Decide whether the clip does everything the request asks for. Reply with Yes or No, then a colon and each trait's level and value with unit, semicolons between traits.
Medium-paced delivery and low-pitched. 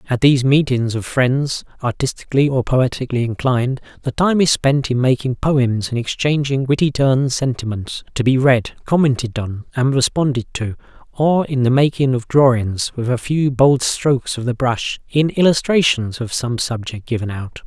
Yes: average, 170 wpm; low, 130 Hz